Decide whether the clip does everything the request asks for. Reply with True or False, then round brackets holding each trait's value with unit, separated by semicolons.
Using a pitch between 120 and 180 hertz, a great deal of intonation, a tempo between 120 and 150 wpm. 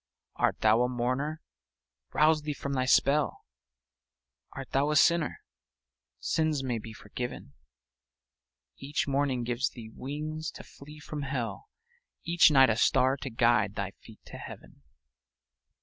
False (135 Hz; 3.8 semitones; 135 wpm)